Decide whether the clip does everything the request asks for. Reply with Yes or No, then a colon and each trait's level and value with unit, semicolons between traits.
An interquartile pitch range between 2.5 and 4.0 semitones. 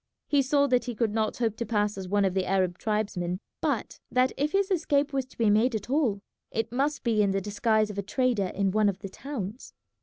No: average, 4.4 semitones